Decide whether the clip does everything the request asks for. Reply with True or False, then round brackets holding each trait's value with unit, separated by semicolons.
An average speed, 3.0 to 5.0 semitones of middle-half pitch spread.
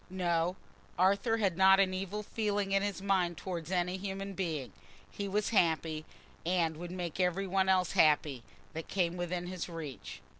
False (165 wpm; 2.4 semitones)